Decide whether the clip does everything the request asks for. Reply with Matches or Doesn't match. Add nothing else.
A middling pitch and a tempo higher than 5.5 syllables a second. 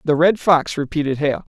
Doesn't match